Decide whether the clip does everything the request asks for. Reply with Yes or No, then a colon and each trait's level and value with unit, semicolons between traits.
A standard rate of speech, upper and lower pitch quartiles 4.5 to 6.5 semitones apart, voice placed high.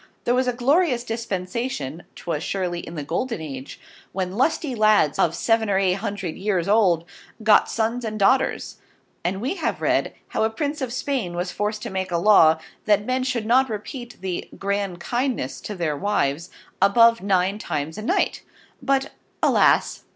Yes: average, 175 wpm; average, 5.2 semitones; high, 205 Hz